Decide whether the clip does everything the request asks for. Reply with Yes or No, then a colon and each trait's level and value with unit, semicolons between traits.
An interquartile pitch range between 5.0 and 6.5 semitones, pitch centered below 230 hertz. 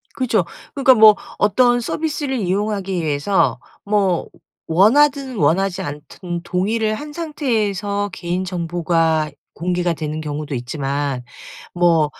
Yes: average, 5.3 semitones; medium, 185 Hz